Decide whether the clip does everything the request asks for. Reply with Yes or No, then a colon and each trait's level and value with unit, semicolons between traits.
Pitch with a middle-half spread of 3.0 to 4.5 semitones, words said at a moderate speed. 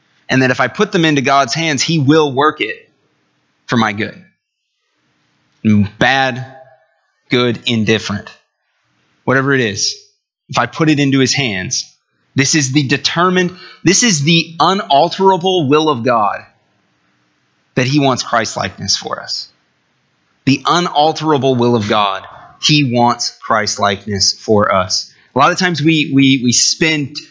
No: average, 5.2 semitones; average, 145 wpm